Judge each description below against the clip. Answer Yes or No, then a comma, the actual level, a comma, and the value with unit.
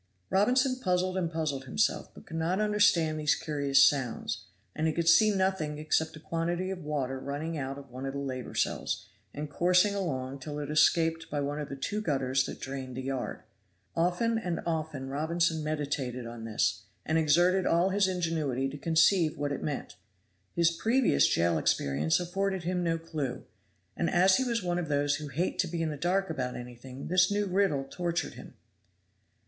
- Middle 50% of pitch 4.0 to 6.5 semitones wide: Yes, average, 4.5 semitones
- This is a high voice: No, medium, 160 Hz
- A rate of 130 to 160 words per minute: No, average, 185 wpm